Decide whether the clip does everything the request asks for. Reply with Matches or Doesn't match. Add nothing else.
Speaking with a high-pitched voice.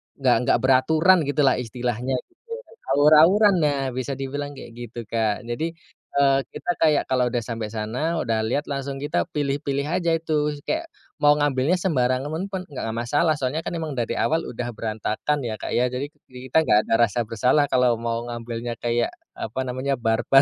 Doesn't match